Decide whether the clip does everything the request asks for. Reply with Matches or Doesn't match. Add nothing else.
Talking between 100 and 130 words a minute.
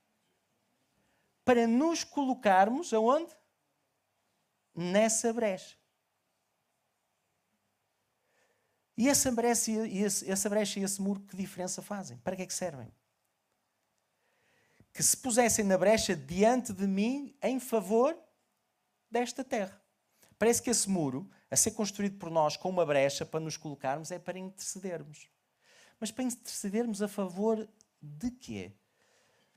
Matches